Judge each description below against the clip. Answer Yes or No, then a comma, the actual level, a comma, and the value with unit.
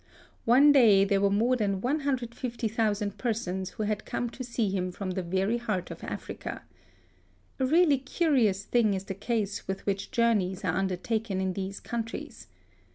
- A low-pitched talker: No, high, 215 Hz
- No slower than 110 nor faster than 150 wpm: No, average, 165 wpm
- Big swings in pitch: No, average, 3.8 semitones